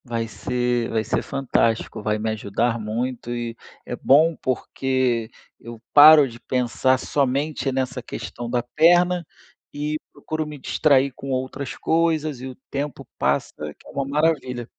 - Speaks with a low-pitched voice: Yes, low, 130 Hz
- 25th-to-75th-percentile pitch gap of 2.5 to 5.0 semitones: Yes, average, 3.6 semitones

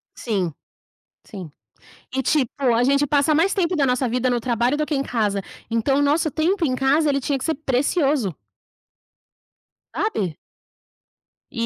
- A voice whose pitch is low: No, very high, 270 Hz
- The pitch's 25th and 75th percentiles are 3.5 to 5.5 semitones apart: Yes, average, 4.2 semitones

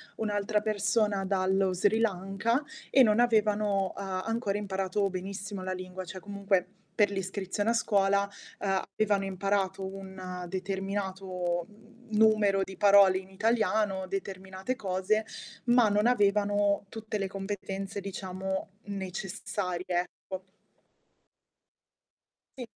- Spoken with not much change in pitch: Yes, narrow, 1.6 semitones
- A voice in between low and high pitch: No, high, 195 Hz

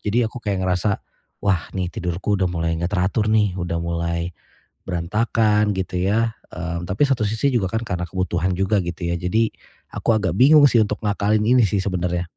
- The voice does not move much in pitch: No, average, 3.7 semitones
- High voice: No, very low, 95 Hz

